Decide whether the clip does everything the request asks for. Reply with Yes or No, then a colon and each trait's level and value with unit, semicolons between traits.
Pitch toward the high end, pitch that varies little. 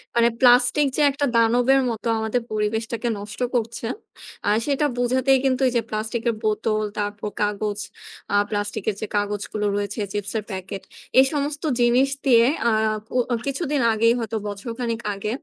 No: high, 225 Hz; average, 3.0 semitones